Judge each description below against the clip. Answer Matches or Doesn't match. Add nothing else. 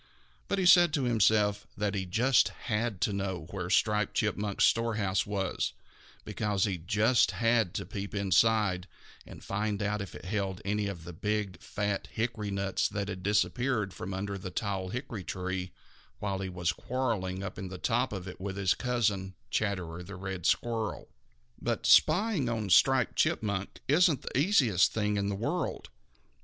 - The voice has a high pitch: Doesn't match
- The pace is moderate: Matches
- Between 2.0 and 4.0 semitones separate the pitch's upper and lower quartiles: Matches